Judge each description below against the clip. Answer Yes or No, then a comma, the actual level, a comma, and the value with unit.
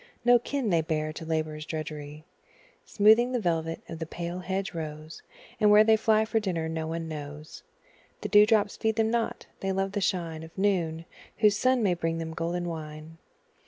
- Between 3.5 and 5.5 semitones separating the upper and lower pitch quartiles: Yes, average, 4.6 semitones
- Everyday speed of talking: Yes, average, 190 wpm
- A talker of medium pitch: Yes, medium, 170 Hz